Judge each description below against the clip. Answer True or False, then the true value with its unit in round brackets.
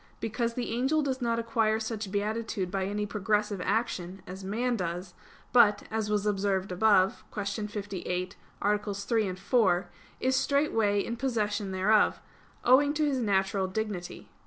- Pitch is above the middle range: True (210 Hz)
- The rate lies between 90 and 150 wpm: True (145 wpm)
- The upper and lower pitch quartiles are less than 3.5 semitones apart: True (3.0 semitones)